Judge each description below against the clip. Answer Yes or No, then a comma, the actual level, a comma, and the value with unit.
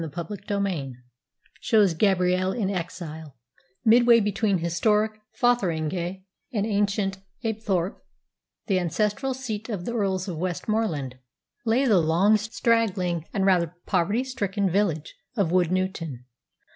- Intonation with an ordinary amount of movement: Yes, average, 3.8 semitones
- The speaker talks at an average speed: No, slow, 115 wpm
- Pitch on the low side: No, high, 195 Hz